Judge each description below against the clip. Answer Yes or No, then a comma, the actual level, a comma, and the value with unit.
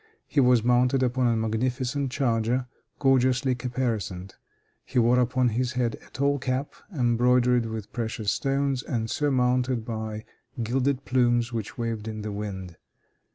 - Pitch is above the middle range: No, low, 125 Hz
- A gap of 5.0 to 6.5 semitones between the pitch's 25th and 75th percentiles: No, narrow, 2.4 semitones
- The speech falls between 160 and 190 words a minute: No, average, 140 wpm